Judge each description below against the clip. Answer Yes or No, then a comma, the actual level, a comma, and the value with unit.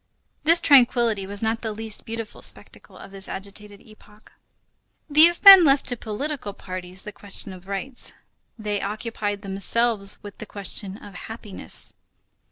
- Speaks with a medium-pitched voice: No, high, 210 Hz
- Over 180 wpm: No, average, 145 wpm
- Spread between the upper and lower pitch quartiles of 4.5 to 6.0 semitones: No, average, 3.1 semitones